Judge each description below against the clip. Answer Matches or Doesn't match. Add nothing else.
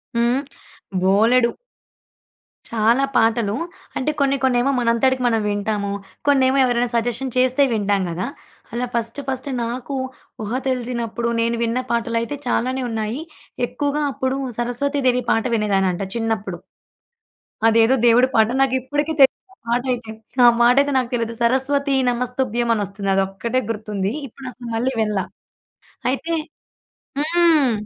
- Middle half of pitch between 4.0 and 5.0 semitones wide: Doesn't match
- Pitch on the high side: Matches